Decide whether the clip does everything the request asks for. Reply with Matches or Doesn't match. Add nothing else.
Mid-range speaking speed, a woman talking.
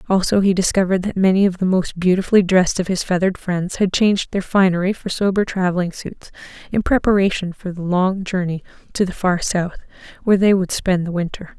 Matches